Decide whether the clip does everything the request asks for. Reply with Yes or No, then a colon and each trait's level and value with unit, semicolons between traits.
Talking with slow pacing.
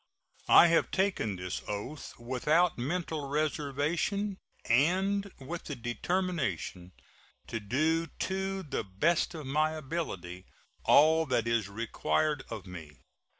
Yes: slow, 115 wpm